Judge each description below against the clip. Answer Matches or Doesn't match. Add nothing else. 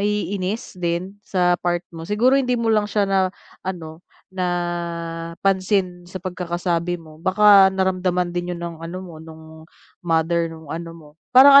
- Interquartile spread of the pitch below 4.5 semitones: Matches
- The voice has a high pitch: Doesn't match